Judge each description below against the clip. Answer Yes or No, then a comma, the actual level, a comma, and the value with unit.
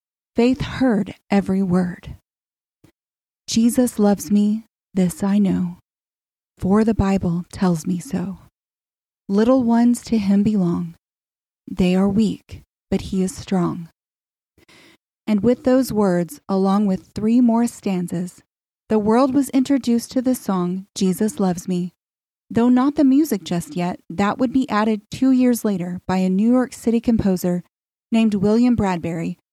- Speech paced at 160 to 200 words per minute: No, average, 140 wpm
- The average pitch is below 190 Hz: No, high, 205 Hz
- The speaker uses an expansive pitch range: No, average, 4.2 semitones